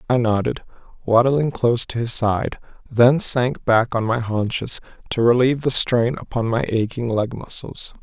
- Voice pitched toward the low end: Yes, low, 120 Hz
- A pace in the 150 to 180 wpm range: Yes, average, 165 wpm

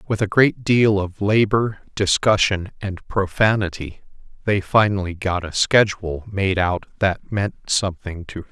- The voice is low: Yes, low, 100 Hz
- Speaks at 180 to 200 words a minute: No, average, 150 wpm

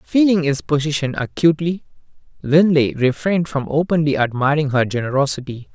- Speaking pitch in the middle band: Yes, medium, 150 Hz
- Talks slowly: Yes, slow, 115 wpm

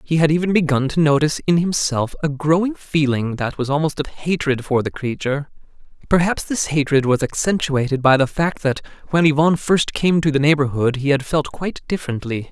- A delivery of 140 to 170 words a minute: No, average, 190 wpm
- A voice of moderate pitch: Yes, medium, 150 Hz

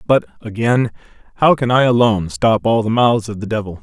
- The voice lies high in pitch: No, low, 110 Hz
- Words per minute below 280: Yes, fast, 205 wpm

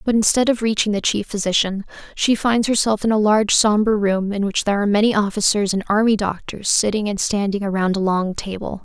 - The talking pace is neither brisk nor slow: No, fast, 210 wpm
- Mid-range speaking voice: No, high, 205 Hz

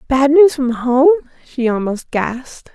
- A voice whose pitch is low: No, very high, 265 Hz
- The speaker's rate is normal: Yes, average, 155 wpm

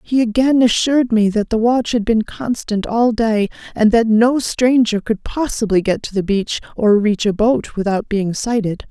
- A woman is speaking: Yes, female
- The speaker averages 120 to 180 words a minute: No, average, 195 wpm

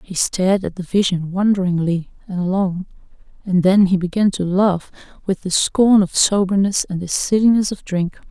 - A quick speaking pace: No, average, 175 wpm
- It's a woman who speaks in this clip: Yes, female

